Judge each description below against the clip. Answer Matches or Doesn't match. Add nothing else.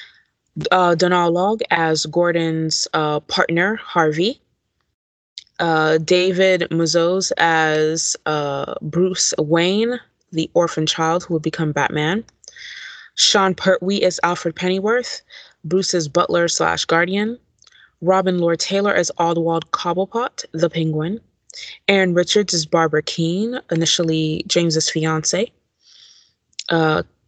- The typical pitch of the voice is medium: Matches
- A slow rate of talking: Matches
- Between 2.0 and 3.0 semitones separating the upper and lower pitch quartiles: Matches